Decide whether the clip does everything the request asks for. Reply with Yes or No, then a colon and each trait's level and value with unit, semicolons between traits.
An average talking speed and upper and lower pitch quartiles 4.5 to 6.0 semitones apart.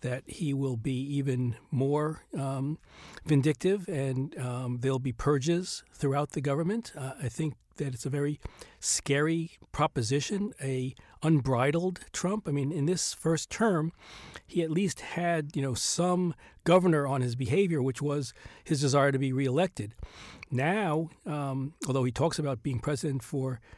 No: average, 150 wpm; average, 3.5 semitones